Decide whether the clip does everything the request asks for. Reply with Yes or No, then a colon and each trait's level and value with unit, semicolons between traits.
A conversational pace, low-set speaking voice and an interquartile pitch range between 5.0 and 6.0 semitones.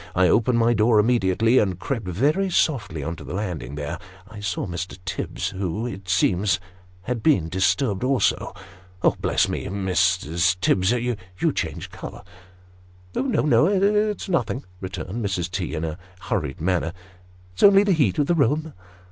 Yes: average, 165 wpm; very low, 95 Hz; wide, 5.4 semitones